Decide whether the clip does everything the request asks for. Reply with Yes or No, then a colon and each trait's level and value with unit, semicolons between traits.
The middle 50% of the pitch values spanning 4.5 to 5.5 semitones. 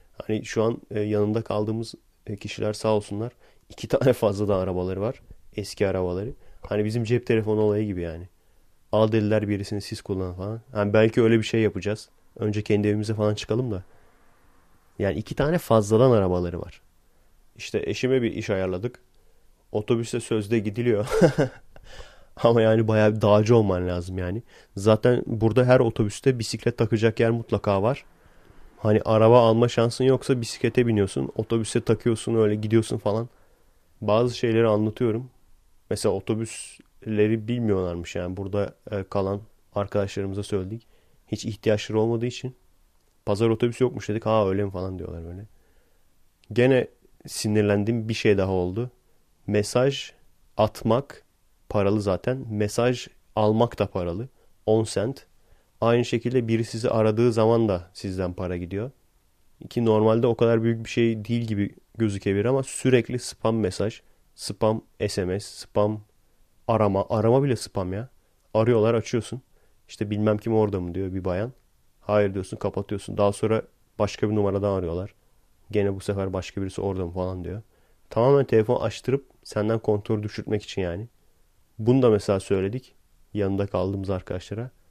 No: average, 2.8 semitones